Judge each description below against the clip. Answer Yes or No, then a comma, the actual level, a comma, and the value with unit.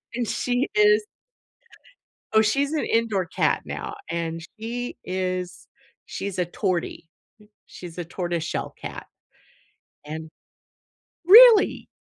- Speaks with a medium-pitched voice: No, high, 200 Hz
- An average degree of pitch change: No, wide, 6.1 semitones